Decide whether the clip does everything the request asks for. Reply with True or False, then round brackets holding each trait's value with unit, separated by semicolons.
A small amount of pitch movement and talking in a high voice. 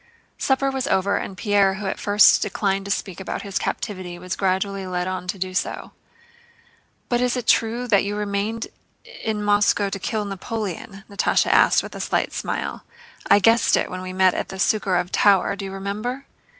True (1.9 semitones; 200 Hz)